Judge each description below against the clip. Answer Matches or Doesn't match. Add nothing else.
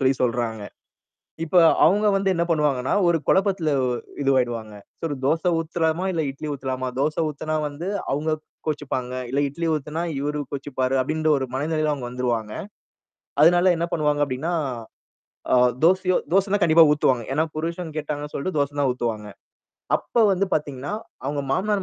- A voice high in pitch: Doesn't match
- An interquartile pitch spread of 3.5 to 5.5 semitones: Matches